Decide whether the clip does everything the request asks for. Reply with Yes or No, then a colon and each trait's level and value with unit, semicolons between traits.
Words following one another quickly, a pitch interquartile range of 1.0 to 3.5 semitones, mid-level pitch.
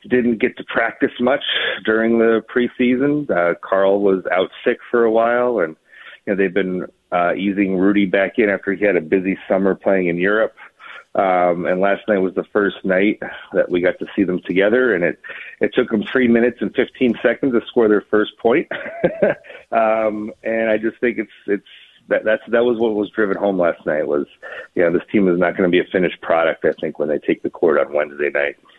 No: fast, 215 wpm; average, 3.1 semitones; low, 100 Hz